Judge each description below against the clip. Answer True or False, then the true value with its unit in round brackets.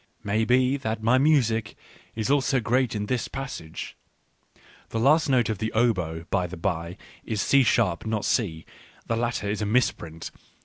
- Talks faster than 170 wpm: False (165 wpm)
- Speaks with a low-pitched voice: True (110 Hz)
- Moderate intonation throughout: True (4.1 semitones)